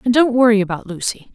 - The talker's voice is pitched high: Yes, high, 225 Hz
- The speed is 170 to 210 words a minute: No, fast, 225 wpm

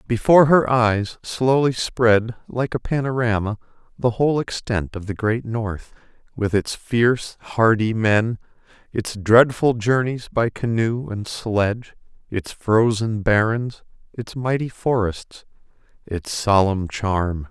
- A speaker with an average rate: No, slow, 125 wpm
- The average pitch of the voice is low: Yes, low, 115 Hz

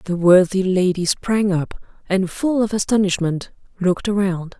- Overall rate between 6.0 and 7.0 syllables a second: No, 4.7 syllables/s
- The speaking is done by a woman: Yes, female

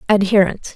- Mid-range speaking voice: No, high, 195 Hz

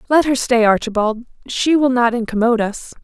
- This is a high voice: Yes, high, 240 Hz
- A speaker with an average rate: Yes, average, 180 wpm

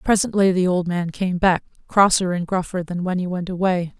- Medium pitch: Yes, medium, 180 Hz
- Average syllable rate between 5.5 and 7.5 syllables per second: No, 5.2 syllables/s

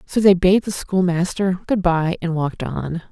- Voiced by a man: No, female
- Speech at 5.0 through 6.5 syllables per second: No, 4.6 syllables/s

